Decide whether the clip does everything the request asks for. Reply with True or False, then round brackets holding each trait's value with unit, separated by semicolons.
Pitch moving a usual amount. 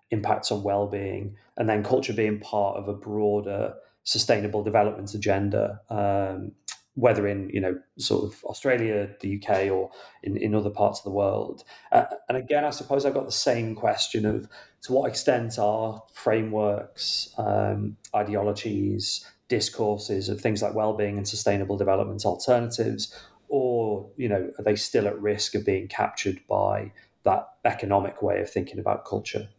False (1.7 semitones)